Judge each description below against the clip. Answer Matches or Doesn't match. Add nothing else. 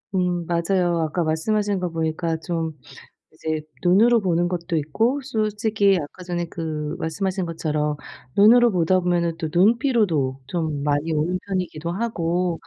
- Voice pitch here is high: Doesn't match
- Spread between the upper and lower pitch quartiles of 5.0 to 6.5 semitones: Doesn't match